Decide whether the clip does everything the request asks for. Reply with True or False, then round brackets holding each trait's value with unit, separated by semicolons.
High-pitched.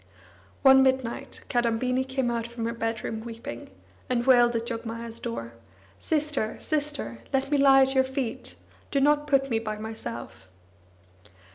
True (240 Hz)